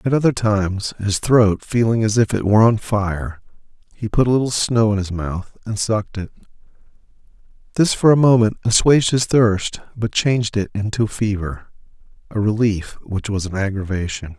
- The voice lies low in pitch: Yes, low, 105 Hz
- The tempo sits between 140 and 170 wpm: Yes, average, 165 wpm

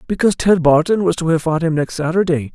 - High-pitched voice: No, medium, 165 Hz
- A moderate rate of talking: No, fast, 235 wpm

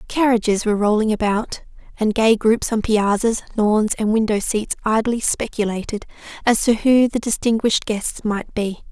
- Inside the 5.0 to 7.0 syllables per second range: No, 4.8 syllables/s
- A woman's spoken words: Yes, female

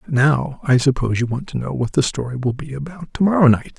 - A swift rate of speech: Yes, fast, 270 wpm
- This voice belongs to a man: Yes, male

